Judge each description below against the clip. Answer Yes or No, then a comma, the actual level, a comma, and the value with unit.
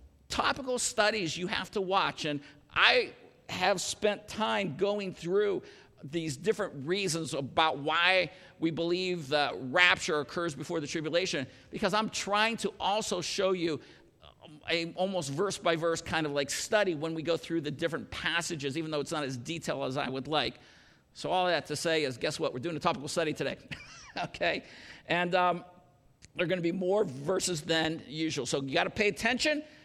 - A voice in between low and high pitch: Yes, medium, 170 Hz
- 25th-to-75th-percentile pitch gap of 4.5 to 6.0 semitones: No, average, 3.7 semitones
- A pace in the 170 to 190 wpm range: Yes, average, 185 wpm